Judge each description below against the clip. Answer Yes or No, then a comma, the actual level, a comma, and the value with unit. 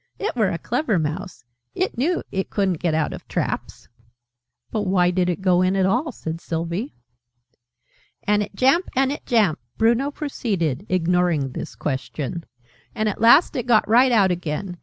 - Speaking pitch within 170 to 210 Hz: Yes, high, 190 Hz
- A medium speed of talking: Yes, average, 175 wpm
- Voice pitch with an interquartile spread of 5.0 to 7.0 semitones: Yes, wide, 5.6 semitones